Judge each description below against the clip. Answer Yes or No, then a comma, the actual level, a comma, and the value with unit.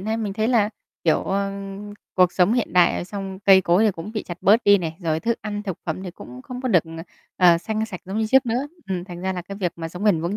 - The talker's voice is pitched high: Yes, high, 195 Hz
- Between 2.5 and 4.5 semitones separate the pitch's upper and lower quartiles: Yes, average, 3.7 semitones